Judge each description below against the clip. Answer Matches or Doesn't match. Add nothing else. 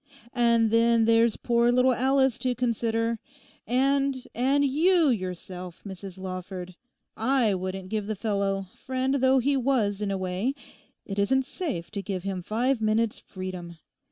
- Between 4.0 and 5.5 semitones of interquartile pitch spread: Matches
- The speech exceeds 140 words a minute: Doesn't match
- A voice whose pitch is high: Matches